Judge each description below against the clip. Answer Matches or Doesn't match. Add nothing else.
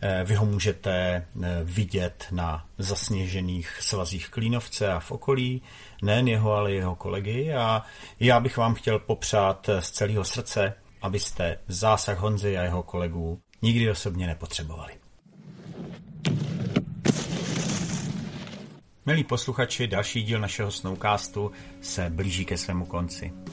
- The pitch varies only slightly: Doesn't match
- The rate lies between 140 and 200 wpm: Doesn't match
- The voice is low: Matches